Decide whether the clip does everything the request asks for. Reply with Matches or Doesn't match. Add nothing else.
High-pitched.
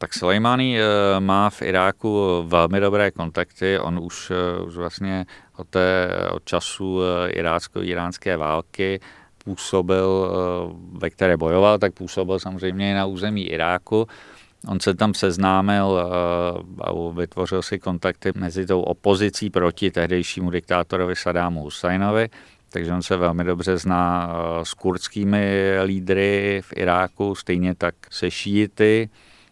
Doesn't match